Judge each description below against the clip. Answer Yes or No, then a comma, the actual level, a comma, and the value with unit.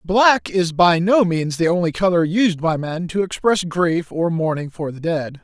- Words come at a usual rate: No, fast, 210 wpm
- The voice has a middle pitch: Yes, medium, 175 Hz